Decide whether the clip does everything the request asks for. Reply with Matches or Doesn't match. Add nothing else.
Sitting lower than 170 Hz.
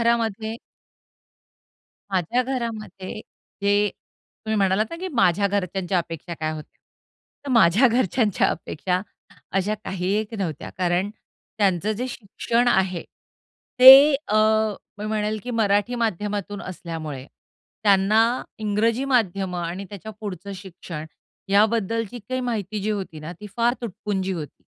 Doesn't match